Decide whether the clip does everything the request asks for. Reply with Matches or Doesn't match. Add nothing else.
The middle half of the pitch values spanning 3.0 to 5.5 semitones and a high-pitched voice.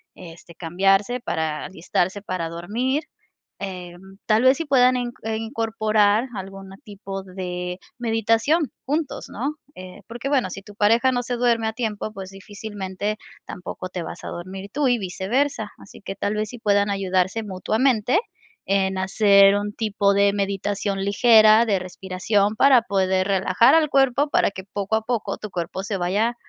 Matches